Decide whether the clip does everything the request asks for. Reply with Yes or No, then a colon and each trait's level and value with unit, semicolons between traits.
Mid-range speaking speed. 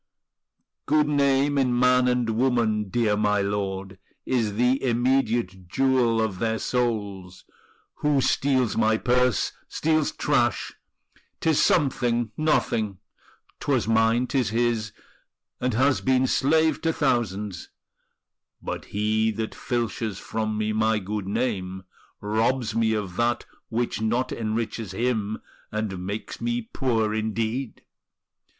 No: slow, 120 wpm